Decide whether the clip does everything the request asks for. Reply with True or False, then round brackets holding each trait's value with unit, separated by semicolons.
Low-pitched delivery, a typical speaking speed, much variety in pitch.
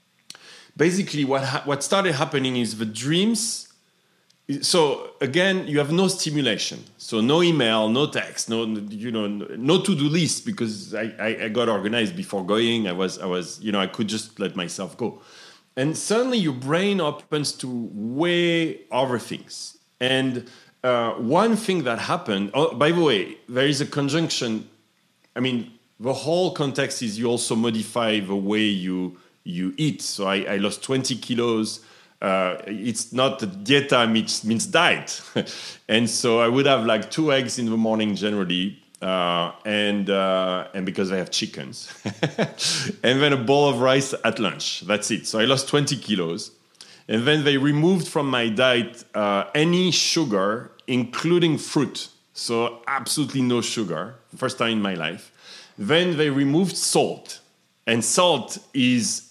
True (130 Hz; 165 wpm; 6.0 semitones)